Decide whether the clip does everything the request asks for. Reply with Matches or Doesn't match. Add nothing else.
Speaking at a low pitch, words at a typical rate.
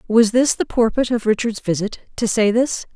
Doesn't match